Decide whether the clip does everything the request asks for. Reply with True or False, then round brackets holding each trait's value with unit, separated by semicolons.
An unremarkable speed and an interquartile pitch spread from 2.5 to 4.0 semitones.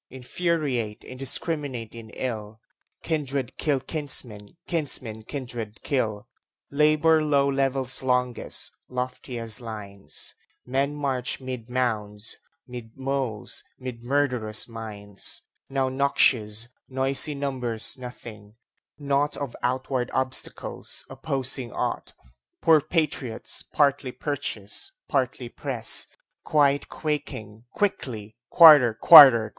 False (95 wpm; 3.7 semitones)